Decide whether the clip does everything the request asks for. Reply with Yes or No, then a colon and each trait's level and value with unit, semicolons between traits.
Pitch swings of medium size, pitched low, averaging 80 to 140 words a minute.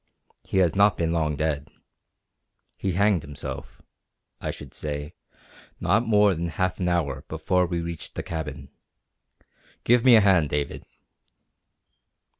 Yes: average, 4.3 semitones; very low, 85 Hz; slow, 135 wpm